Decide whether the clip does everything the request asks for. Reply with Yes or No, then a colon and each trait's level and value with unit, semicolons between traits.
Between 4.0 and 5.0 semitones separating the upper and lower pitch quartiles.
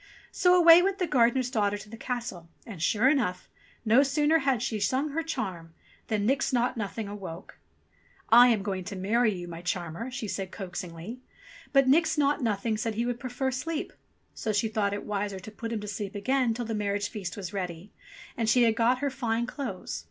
Yes: average, 4.4 semitones